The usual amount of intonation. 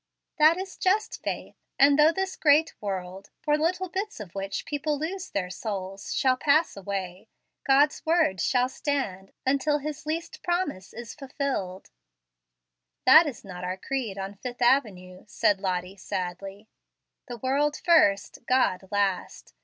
No: wide, 7.7 semitones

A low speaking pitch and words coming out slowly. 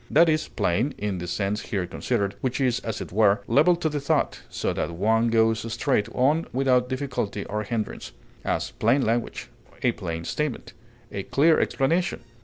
No: low, 115 Hz; average, 175 wpm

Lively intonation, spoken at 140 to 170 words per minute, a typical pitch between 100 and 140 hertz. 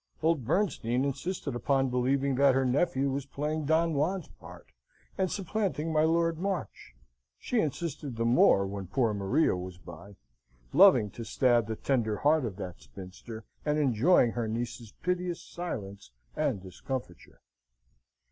Yes: wide, 6.3 semitones; average, 145 wpm; low, 135 Hz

